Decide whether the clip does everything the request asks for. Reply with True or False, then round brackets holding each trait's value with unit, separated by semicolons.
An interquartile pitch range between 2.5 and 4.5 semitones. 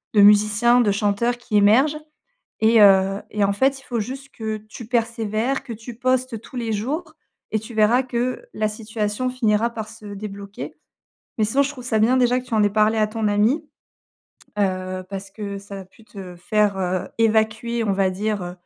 True (2.9 semitones)